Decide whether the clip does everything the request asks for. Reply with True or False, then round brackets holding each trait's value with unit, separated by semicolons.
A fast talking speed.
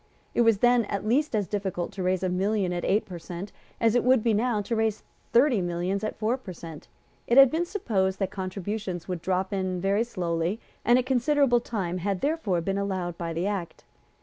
True (210 wpm)